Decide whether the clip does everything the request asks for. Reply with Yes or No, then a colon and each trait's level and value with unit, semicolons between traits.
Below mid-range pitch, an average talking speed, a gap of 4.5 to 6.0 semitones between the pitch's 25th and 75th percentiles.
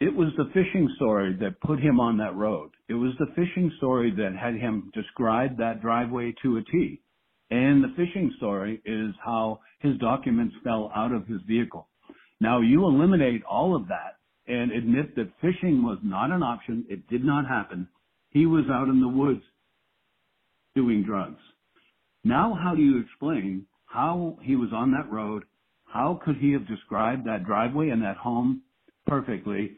Yes: low, 125 Hz; average, 175 wpm; average, 5.3 semitones